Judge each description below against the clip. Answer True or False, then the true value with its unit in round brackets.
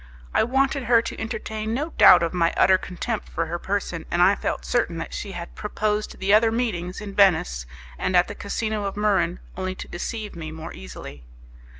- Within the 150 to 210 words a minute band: True (200 wpm)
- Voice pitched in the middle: False (195 Hz)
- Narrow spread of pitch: False (4.0 semitones)